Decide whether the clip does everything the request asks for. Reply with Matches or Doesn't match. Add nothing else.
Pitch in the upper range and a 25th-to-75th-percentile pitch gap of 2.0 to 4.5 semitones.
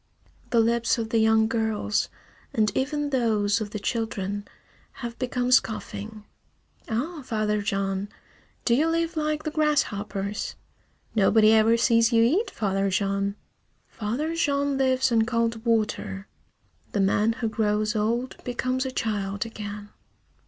Matches